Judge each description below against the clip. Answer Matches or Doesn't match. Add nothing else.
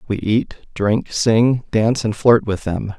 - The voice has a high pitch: Doesn't match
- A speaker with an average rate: Matches